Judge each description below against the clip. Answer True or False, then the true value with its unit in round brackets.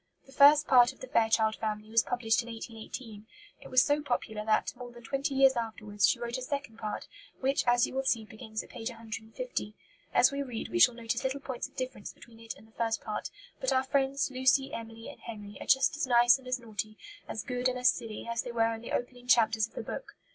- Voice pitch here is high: True (240 Hz)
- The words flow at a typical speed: False (235 wpm)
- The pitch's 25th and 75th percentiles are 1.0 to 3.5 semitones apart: True (2.8 semitones)